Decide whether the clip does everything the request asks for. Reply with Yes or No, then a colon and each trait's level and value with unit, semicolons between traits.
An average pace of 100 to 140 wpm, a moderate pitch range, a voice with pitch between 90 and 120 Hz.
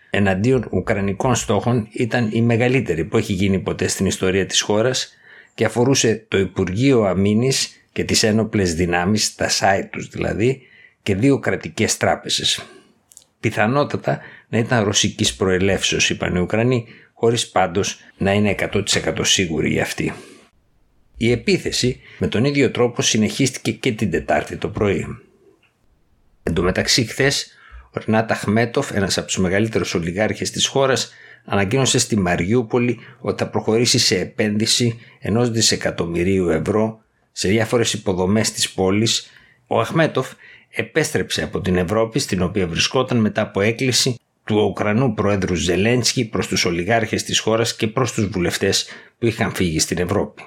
Yes: average, 135 wpm; average, 3.7 semitones; low, 110 Hz